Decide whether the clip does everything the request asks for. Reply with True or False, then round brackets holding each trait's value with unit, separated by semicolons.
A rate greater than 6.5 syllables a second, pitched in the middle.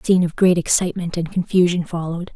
True (7.0 syllables/s; 175 Hz)